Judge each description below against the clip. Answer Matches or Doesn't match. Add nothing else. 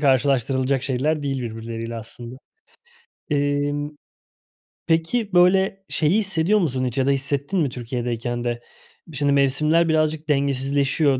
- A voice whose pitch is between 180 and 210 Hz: Doesn't match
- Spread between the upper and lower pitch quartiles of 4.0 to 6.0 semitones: Doesn't match